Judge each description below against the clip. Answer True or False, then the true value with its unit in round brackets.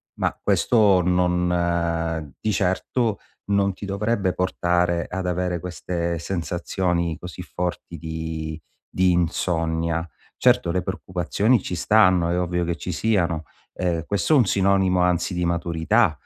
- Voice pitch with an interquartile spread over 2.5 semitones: False (1.8 semitones)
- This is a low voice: True (90 Hz)